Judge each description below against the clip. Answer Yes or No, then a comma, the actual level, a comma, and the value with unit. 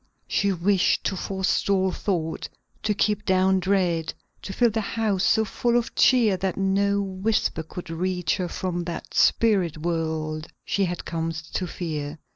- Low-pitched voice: No, high, 190 Hz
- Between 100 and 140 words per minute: No, average, 155 wpm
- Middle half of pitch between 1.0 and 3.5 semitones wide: Yes, average, 2.9 semitones